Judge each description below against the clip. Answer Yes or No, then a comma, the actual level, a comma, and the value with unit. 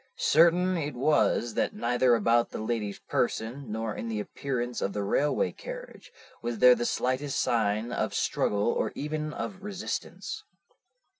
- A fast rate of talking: No, average, 150 wpm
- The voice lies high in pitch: No, low, 125 Hz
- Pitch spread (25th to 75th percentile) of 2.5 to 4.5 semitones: No, average, 5.0 semitones